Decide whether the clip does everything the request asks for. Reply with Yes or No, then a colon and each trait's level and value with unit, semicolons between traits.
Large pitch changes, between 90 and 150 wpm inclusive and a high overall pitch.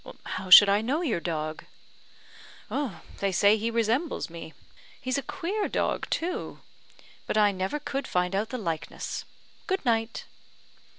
Yes: wide, 6.8 semitones; average, 140 wpm; high, 220 Hz